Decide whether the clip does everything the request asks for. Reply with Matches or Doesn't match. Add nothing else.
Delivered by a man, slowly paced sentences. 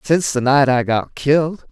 Doesn't match